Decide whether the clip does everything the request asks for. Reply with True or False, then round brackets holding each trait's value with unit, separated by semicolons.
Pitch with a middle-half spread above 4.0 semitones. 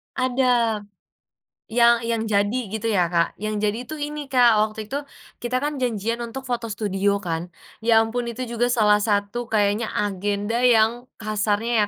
False (2.7 semitones)